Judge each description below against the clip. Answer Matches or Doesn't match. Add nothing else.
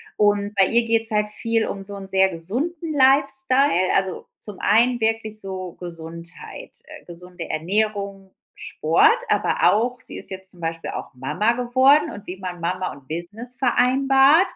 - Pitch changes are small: Doesn't match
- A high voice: Matches